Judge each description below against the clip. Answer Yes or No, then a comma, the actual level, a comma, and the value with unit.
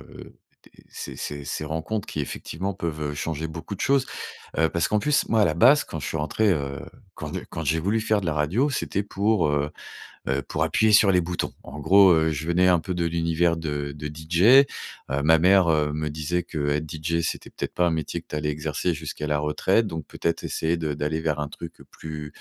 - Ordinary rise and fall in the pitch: Yes, average, 3.4 semitones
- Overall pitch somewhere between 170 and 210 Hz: No, very low, 80 Hz